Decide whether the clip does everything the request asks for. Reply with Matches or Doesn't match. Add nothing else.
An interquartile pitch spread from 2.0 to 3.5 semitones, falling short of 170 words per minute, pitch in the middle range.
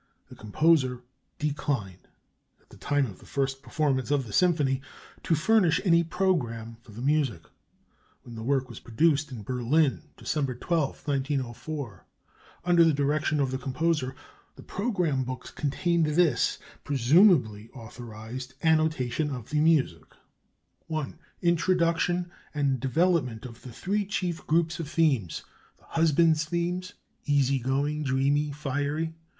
Doesn't match